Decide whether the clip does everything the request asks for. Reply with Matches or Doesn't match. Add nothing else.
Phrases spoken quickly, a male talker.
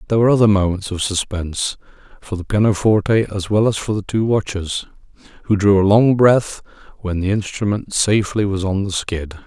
Doesn't match